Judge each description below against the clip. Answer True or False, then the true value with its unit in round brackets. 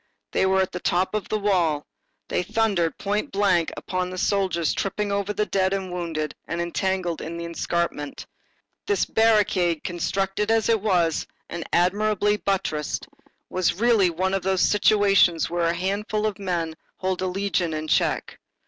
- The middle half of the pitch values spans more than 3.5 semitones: False (2.9 semitones)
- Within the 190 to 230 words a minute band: False (165 wpm)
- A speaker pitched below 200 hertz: True (190 Hz)